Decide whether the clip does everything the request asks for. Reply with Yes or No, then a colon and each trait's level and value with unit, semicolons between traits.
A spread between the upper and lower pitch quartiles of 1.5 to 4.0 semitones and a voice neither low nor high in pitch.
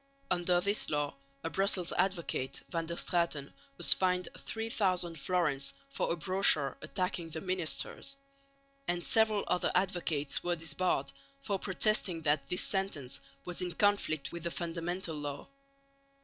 Yes: average, 2.8 semitones; medium, 175 Hz